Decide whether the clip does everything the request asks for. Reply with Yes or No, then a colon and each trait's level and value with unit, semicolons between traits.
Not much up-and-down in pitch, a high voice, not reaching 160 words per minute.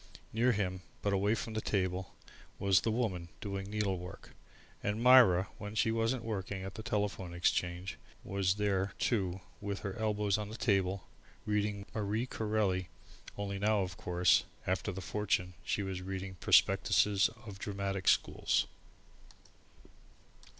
No: narrow, 2.1 semitones; low, 100 Hz; average, 145 wpm